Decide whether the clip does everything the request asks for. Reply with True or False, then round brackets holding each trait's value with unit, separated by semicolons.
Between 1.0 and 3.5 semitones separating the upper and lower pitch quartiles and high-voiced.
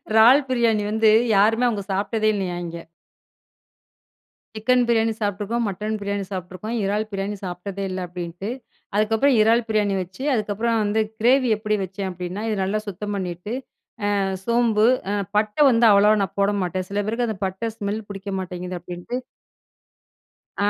True (2.8 semitones; 205 Hz)